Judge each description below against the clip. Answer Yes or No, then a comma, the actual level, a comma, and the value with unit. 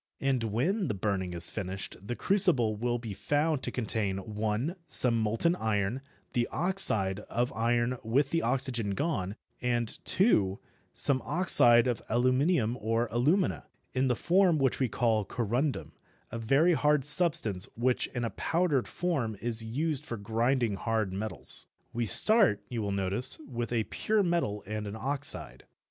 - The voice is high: No, low, 120 Hz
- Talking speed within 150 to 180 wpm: Yes, average, 155 wpm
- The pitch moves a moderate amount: Yes, average, 4.8 semitones